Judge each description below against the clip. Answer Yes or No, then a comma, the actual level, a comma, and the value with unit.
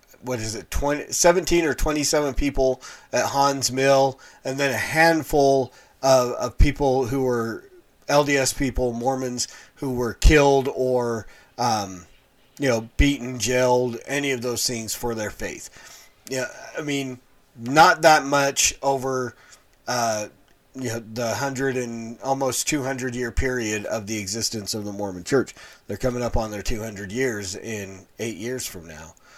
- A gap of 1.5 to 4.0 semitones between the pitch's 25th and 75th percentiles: Yes, average, 3.3 semitones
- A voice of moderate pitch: No, low, 130 Hz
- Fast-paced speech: No, average, 150 wpm